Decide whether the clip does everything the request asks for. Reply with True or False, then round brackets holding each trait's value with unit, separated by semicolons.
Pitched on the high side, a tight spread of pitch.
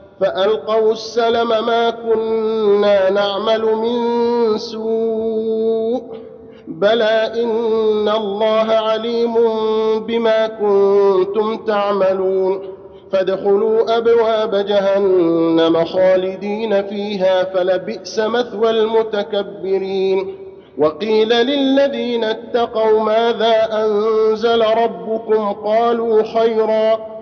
True (220 Hz; 2.1 semitones)